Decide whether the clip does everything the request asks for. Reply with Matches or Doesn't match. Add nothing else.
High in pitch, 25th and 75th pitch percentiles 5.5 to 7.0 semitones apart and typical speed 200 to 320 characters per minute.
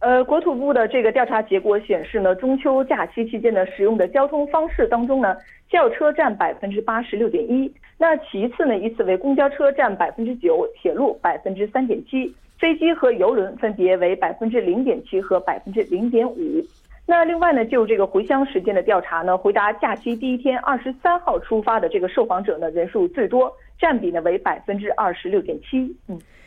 Matches